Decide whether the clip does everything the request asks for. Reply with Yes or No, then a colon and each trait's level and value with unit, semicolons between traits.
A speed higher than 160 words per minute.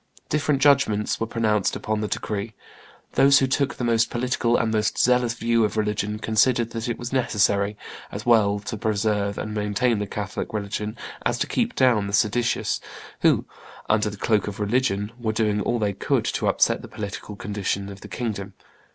Yes: average, 185 wpm